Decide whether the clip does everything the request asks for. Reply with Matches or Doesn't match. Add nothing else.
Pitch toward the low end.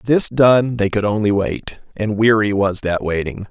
Matches